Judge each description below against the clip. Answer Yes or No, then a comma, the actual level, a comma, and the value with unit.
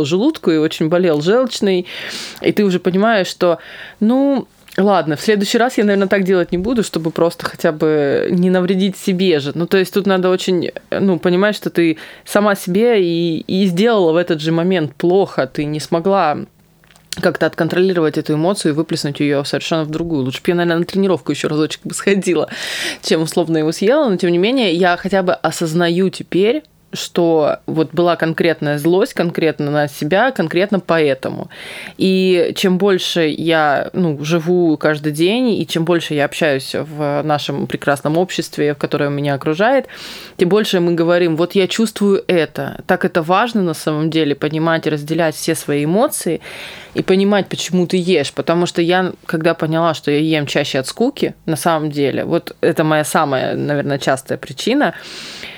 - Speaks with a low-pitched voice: No, medium, 170 Hz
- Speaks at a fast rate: Yes, fast, 175 wpm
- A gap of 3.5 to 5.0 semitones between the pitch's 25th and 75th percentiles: No, average, 3.1 semitones